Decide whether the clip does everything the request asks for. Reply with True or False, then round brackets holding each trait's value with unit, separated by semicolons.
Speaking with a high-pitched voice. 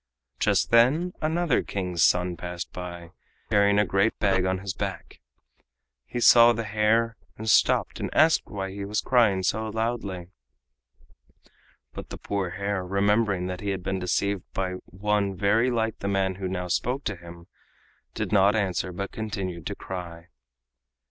False (100 Hz)